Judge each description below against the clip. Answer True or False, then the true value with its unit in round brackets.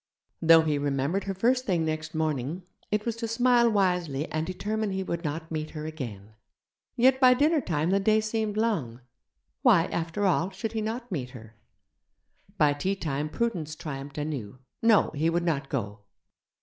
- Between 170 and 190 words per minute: True (175 wpm)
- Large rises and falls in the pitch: True (6.6 semitones)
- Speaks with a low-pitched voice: False (170 Hz)